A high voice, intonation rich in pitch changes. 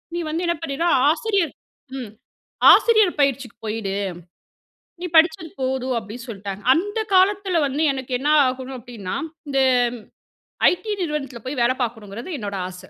Yes: very high, 265 Hz; wide, 6.1 semitones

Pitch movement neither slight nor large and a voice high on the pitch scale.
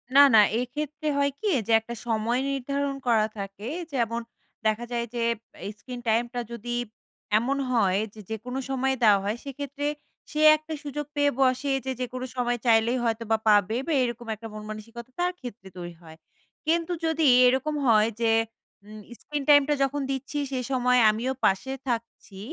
Yes: average, 3.9 semitones; high, 245 Hz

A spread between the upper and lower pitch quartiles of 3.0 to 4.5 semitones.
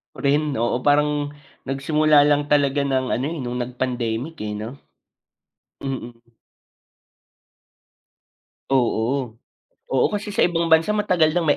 Yes: average, 3.6 semitones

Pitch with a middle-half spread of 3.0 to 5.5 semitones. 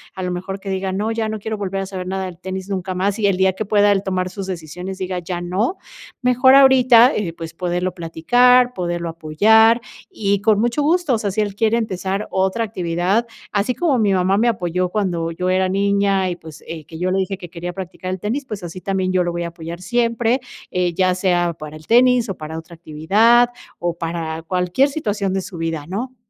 Yes: average, 3.7 semitones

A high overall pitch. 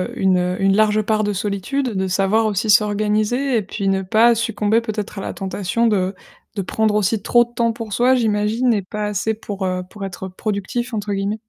Yes: high, 210 Hz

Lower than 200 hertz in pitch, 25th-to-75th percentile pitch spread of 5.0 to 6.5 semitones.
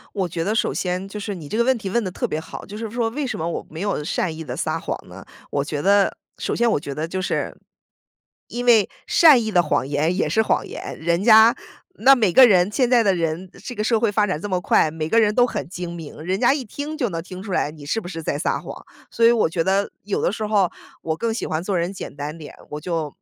Yes: high, 190 Hz; wide, 5.4 semitones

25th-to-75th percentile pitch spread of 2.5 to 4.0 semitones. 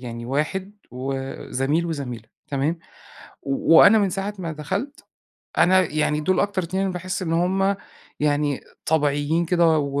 No: average, 4.6 semitones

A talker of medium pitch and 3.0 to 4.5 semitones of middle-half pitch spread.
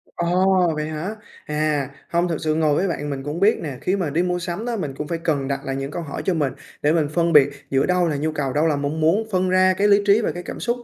Yes: medium, 160 Hz; average, 3.8 semitones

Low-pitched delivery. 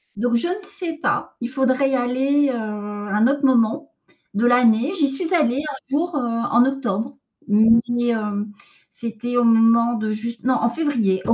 No: high, 245 Hz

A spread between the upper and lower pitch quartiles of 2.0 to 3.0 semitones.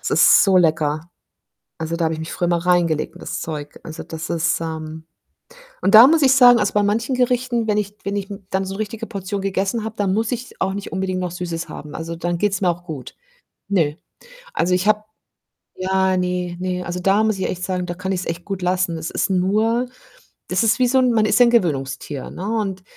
No: average, 3.6 semitones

